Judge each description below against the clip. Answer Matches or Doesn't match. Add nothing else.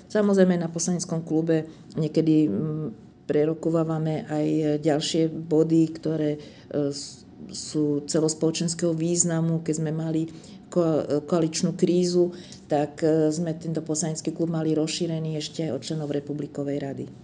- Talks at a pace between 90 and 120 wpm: Matches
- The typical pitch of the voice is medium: Matches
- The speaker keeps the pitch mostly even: Matches